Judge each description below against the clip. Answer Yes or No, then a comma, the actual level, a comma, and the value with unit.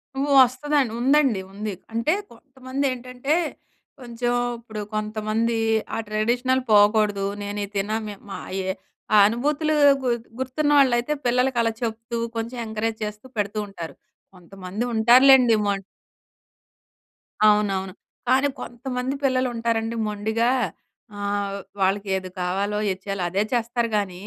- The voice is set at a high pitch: Yes, high, 230 Hz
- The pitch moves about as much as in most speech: Yes, average, 3.6 semitones